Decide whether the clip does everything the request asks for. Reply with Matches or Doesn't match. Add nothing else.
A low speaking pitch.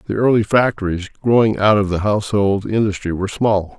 Matches